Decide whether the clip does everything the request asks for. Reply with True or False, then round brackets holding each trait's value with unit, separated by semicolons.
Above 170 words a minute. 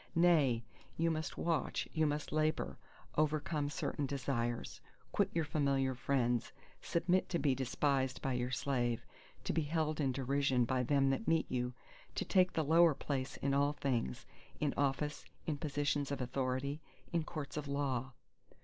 False (160 wpm)